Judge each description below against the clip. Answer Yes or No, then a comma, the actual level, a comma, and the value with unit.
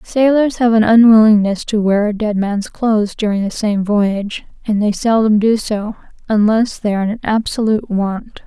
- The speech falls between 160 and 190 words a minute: Yes, average, 175 wpm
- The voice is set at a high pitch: Yes, high, 215 Hz